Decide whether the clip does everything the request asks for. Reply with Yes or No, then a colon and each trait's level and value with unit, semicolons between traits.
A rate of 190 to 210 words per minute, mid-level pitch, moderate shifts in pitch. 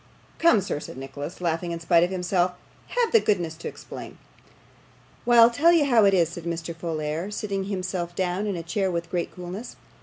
Yes: average, 200 wpm; medium, 180 Hz; average, 3.3 semitones